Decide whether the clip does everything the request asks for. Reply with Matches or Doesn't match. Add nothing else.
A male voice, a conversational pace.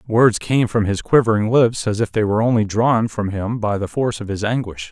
Doesn't match